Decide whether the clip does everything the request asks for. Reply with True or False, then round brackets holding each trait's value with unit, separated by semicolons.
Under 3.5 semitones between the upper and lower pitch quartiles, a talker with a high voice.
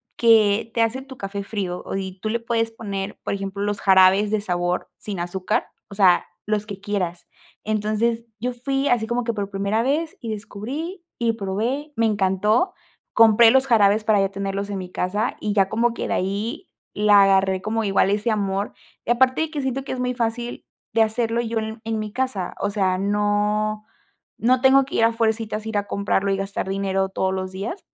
True (2.8 semitones; 215 Hz)